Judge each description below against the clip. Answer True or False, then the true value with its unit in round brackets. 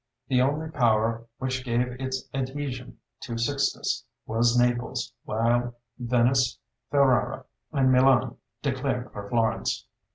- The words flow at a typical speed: False (110 wpm)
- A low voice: True (125 Hz)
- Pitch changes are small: True (2.0 semitones)